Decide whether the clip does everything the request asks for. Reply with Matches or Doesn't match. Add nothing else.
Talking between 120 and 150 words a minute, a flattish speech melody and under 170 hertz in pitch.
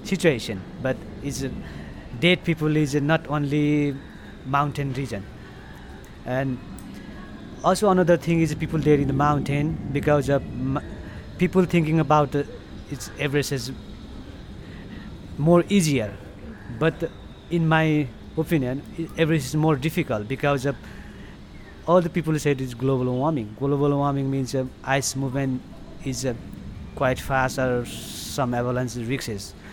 Doesn't match